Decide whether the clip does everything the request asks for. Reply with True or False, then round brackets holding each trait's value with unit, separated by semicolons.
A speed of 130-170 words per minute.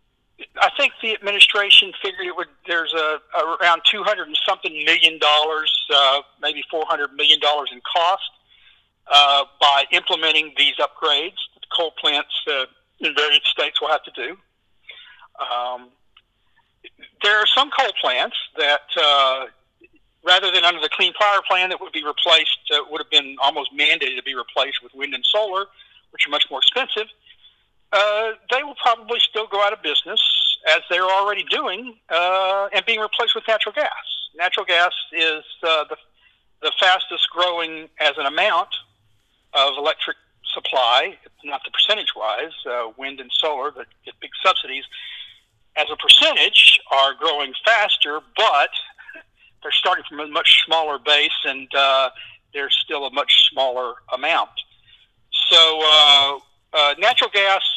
True (155 wpm)